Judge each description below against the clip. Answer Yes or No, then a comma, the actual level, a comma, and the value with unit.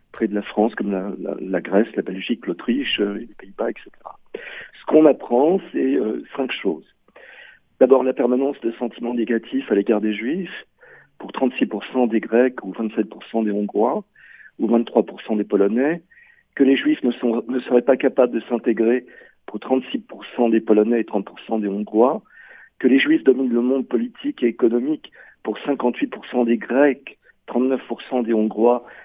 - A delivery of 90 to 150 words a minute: No, average, 165 wpm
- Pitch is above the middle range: No, low, 120 Hz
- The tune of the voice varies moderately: Yes, average, 3.0 semitones